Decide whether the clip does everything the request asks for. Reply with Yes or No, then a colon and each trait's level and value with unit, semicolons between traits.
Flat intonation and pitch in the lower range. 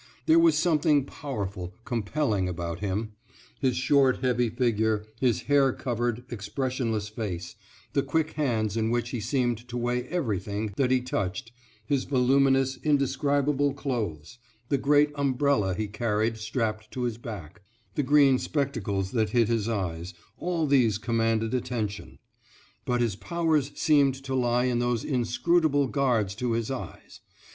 No: average, 4.2 semitones; low, 120 Hz